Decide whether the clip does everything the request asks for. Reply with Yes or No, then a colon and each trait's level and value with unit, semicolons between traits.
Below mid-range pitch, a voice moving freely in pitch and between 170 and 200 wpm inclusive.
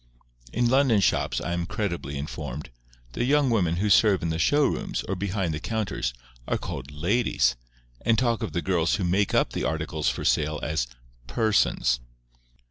Yes: very low, 90 Hz; wide, 6.1 semitones; average, 175 wpm